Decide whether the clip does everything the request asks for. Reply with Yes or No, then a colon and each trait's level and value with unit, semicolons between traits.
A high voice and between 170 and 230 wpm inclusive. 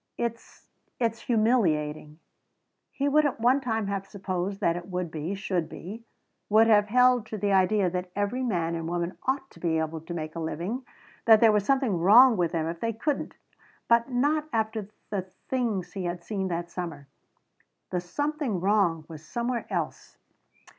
Yes: high, 200 Hz; average, 175 wpm